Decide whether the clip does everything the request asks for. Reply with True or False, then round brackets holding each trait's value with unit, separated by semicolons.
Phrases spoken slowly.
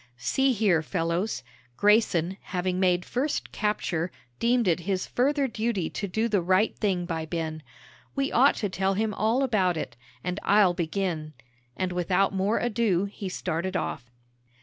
False (155 wpm)